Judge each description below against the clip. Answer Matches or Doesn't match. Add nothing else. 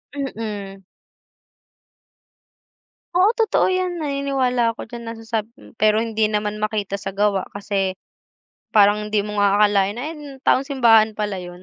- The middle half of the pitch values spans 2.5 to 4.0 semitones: Matches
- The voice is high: Matches